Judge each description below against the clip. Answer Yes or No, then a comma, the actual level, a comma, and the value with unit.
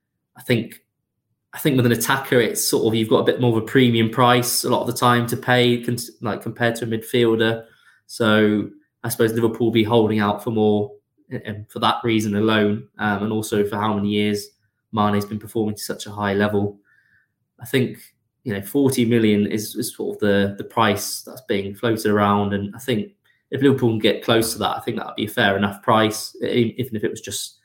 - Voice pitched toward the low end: Yes, low, 110 Hz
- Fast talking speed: Yes, fast, 225 wpm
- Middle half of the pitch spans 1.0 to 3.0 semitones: Yes, narrow, 2.4 semitones